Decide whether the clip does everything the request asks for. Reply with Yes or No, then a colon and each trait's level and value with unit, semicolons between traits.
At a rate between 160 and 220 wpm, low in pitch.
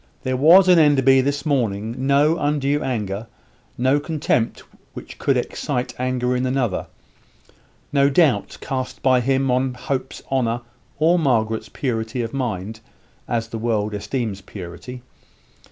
No: slow, 135 wpm; low, 130 Hz